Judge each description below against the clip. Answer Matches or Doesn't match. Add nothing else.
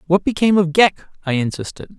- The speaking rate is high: Doesn't match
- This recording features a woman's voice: Doesn't match